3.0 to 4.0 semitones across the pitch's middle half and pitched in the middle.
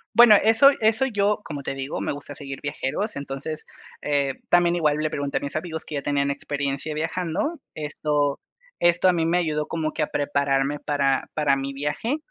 Yes: average, 3.5 semitones; medium, 150 Hz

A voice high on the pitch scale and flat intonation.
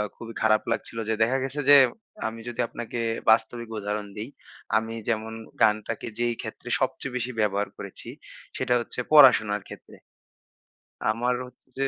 No: low, 115 Hz; narrow, 2.2 semitones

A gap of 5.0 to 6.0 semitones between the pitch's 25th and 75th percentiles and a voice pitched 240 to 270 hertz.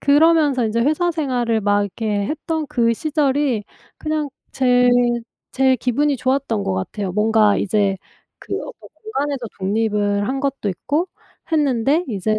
Yes: wide, 5.6 semitones; very high, 250 Hz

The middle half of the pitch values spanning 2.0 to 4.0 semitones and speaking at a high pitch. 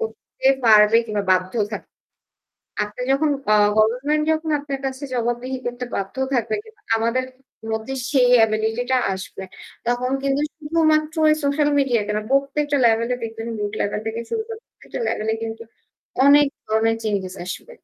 No: average, 4.4 semitones; high, 245 Hz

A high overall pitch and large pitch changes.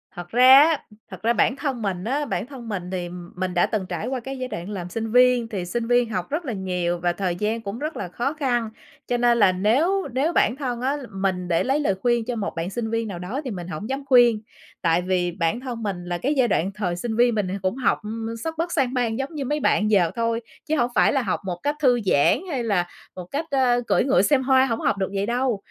Yes: high, 230 Hz; wide, 5.7 semitones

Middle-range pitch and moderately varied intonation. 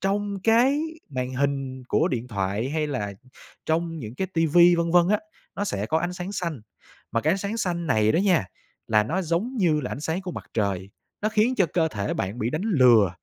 No: medium, 160 Hz; wide, 7.5 semitones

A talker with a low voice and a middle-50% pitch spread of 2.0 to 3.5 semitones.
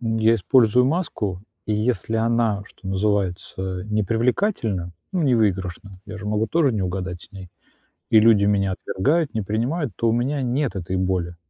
No: low, 105 Hz; average, 4.0 semitones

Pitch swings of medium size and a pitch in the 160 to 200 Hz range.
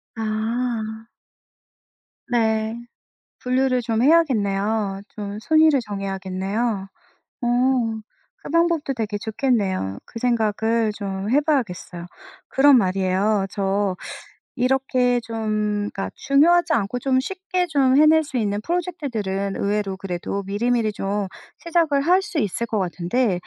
No: average, 5.0 semitones; high, 225 Hz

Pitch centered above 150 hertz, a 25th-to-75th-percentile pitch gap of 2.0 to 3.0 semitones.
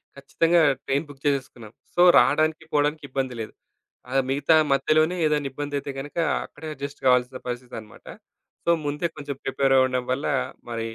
No: medium, 140 Hz; narrow, 2.5 semitones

